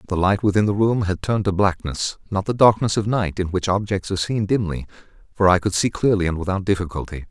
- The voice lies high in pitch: No, low, 100 Hz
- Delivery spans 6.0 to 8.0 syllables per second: Yes, 6.1 syllables/s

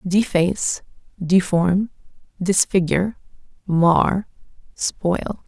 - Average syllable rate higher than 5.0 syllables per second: No, 3.3 syllables/s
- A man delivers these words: No, female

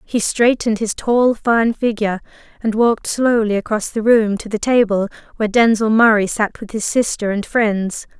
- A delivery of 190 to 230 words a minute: No, average, 175 wpm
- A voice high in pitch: Yes, high, 220 Hz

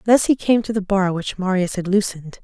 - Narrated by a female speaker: Yes, female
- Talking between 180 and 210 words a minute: No, fast, 245 wpm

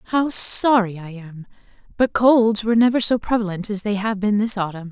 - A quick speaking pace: No, average, 195 wpm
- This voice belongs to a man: No, female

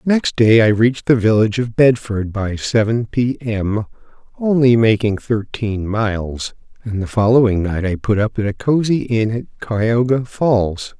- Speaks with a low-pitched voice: Yes, low, 115 Hz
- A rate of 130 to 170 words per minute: Yes, average, 165 wpm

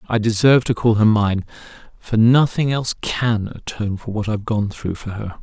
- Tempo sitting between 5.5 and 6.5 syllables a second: No, 5.3 syllables/s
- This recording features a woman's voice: No, male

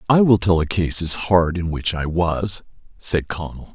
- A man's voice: Yes, male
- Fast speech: Yes, fast, 210 wpm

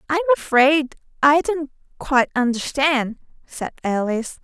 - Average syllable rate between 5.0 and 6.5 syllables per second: No, 4.5 syllables/s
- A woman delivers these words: Yes, female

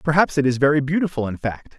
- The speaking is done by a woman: No, male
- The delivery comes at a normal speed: No, fast, 235 wpm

